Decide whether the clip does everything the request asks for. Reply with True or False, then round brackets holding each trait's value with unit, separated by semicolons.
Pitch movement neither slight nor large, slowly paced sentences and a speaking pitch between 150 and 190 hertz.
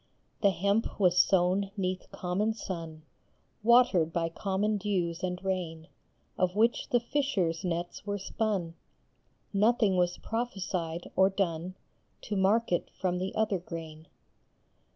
True (3.0 semitones; 130 wpm; 185 Hz)